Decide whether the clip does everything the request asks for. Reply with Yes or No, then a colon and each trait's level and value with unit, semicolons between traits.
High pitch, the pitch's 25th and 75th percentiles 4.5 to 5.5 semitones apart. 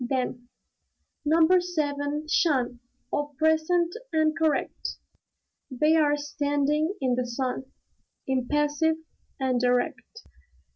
No: very high, 290 Hz; average, 3.3 semitones